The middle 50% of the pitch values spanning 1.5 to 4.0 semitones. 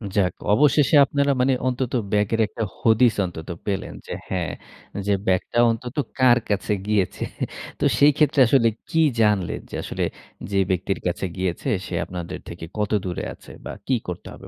No: wide, 5.6 semitones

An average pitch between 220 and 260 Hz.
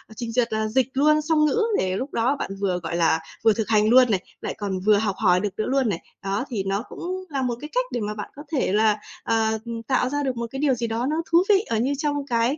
Yes: high, 230 Hz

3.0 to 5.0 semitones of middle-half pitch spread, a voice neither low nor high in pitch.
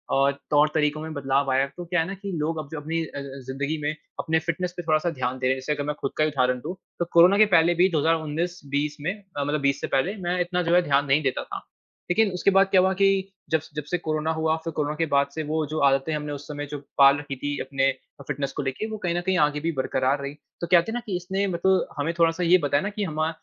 Yes: average, 3.7 semitones; medium, 155 Hz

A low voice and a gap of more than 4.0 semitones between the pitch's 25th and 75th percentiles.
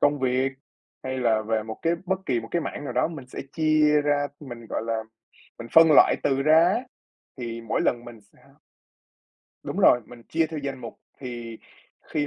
Yes: low, 130 Hz; average, 4.7 semitones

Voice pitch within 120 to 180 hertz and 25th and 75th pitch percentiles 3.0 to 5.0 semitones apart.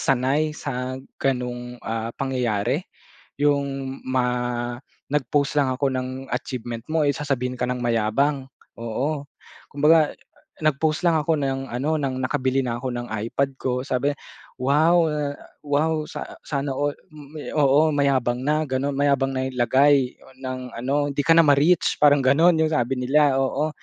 No: low, 135 Hz; narrow, 2.5 semitones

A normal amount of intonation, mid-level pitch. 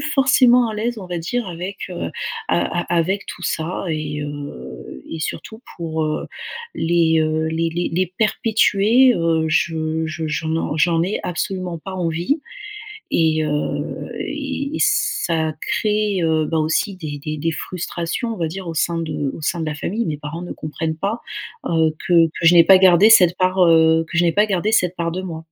Yes: average, 3.3 semitones; medium, 170 Hz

